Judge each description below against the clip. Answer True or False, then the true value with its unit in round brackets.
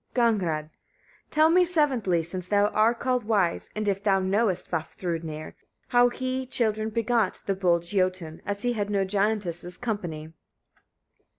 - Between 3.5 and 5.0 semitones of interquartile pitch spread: True (4.6 semitones)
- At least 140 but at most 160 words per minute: True (150 wpm)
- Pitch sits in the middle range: False (205 Hz)